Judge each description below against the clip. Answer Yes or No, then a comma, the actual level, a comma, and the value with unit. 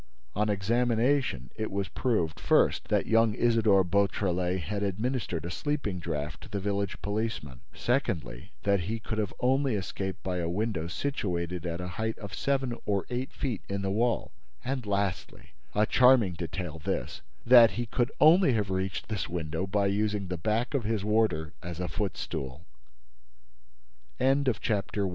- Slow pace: No, average, 150 wpm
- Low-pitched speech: Yes, low, 100 Hz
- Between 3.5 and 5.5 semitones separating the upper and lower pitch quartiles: Yes, average, 4.1 semitones